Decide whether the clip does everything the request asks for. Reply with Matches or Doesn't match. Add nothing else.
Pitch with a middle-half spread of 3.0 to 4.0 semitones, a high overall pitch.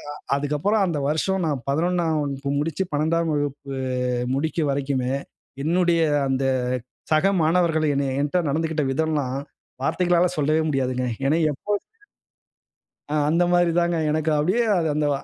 Doesn't match